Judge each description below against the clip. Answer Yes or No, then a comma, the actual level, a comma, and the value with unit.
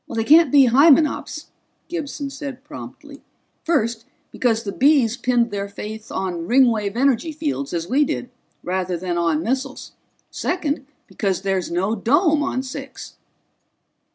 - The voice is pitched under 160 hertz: No, very high, 250 Hz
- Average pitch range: No, wide, 6.2 semitones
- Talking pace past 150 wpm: No, slow, 135 wpm